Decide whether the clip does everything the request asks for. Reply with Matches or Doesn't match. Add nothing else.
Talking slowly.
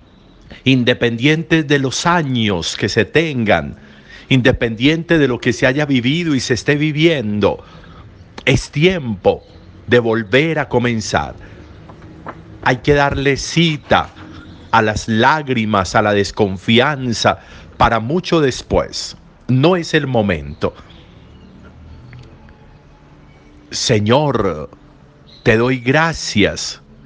Matches